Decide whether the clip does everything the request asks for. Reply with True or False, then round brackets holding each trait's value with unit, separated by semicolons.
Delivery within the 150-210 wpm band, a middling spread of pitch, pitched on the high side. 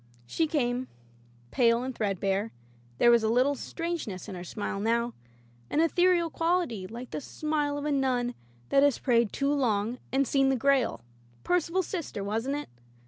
True (170 wpm; 4.6 semitones; 255 Hz)